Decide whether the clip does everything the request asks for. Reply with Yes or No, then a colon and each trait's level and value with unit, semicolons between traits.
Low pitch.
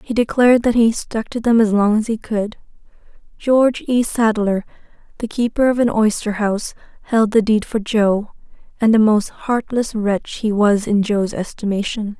No: high, 220 Hz